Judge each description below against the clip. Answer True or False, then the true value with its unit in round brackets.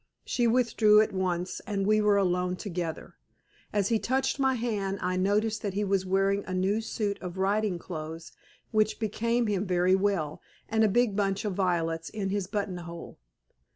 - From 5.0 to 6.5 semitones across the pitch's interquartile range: False (2.7 semitones)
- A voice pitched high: True (200 Hz)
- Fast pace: False (175 wpm)